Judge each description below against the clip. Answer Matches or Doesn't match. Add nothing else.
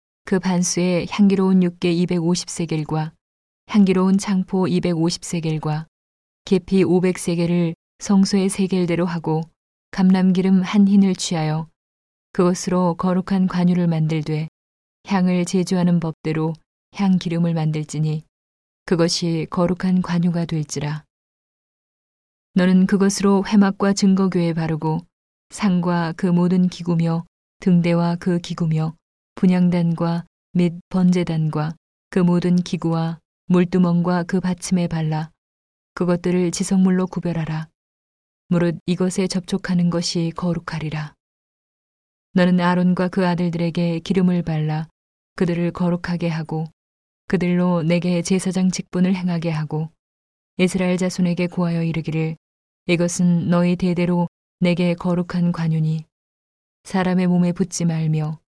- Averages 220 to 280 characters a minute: Matches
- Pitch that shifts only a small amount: Matches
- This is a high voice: Doesn't match